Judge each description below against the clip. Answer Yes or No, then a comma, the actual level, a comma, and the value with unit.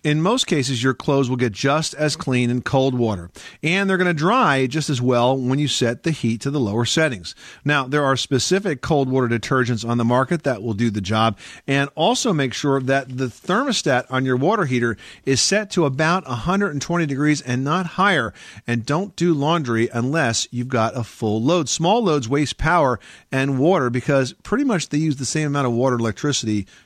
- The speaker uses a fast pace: Yes, fast, 210 wpm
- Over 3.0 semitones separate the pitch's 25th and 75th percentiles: Yes, average, 4.6 semitones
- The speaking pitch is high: No, low, 135 Hz